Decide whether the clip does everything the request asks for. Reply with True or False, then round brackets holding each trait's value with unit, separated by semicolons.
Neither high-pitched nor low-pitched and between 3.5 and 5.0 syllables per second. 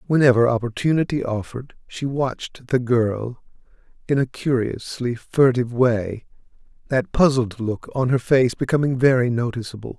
False (125 Hz; 4.9 syllables/s)